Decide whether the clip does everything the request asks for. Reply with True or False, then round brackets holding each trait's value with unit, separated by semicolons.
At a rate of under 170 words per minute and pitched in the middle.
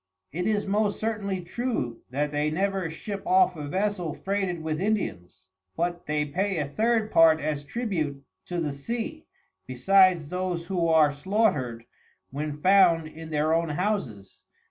True (150 wpm; 170 Hz)